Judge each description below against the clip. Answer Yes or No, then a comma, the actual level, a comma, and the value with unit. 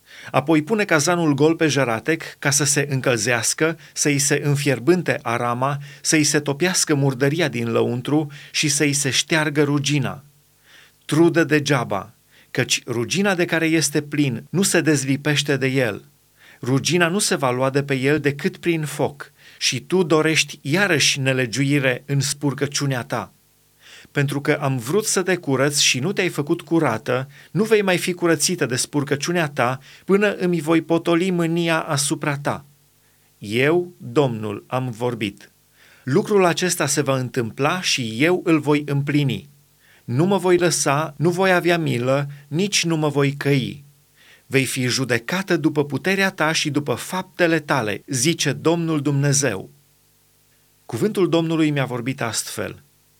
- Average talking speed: Yes, average, 145 wpm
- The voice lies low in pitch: No, medium, 145 Hz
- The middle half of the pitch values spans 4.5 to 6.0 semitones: No, average, 3.4 semitones